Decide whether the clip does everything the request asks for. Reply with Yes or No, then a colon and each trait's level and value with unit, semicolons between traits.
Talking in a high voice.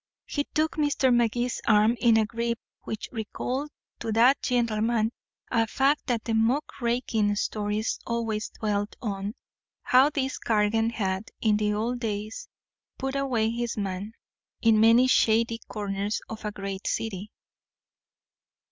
Yes: high, 225 Hz